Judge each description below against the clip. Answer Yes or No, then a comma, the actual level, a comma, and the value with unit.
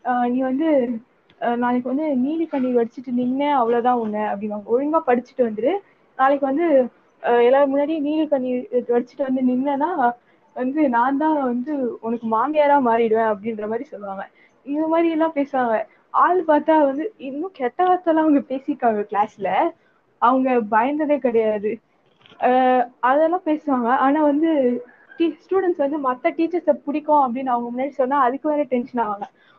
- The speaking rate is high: Yes, fast, 135 wpm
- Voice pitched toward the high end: Yes, very high, 260 Hz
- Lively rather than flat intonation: No, average, 3.7 semitones